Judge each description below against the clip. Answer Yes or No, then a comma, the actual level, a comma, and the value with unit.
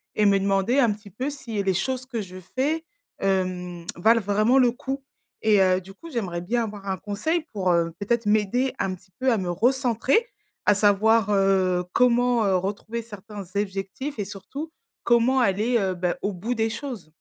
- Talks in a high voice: Yes, high, 210 Hz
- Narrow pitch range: No, average, 4.2 semitones